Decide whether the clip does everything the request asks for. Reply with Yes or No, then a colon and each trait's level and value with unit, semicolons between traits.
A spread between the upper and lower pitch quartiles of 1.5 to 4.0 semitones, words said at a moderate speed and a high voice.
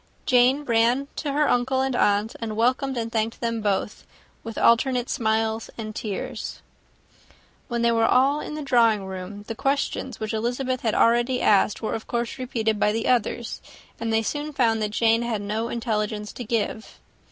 Yes: narrow, 2.5 semitones; average, 175 wpm; high, 230 Hz